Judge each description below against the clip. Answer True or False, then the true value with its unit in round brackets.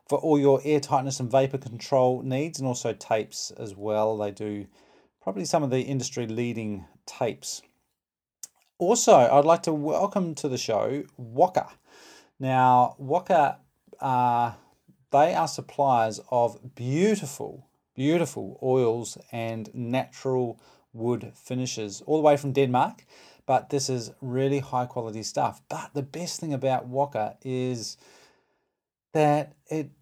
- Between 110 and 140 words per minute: True (135 wpm)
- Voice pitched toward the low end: True (130 Hz)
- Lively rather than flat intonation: False (3.4 semitones)